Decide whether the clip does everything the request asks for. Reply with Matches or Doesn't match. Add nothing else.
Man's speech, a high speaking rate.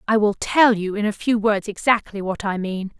Doesn't match